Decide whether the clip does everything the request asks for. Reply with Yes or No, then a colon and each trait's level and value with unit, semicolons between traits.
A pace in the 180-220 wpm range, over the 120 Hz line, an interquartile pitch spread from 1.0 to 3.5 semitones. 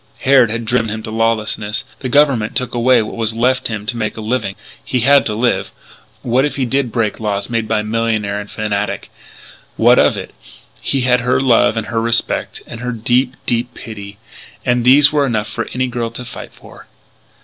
No: average, 200 wpm; low, 115 Hz; narrow, 2.5 semitones